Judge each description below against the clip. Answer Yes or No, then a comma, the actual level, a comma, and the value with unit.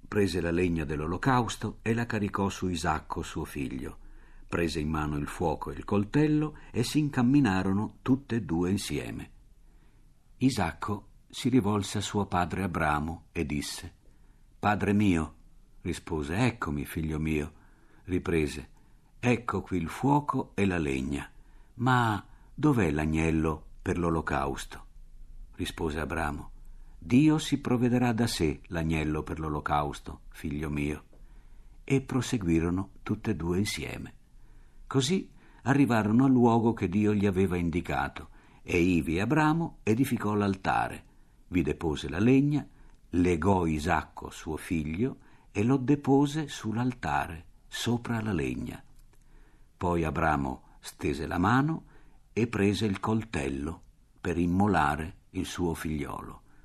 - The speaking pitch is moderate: No, very low, 95 Hz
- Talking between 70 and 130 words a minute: Yes, average, 125 wpm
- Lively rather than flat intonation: Yes, wide, 6.5 semitones